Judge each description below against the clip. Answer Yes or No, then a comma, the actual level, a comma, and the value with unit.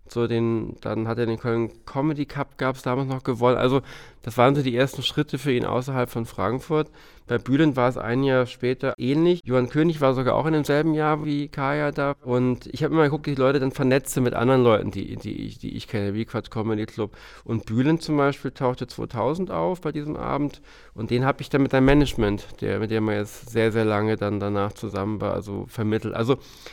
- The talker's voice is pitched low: Yes, low, 125 Hz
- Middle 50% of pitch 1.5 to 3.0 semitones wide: No, average, 3.7 semitones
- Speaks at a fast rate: Yes, fast, 230 wpm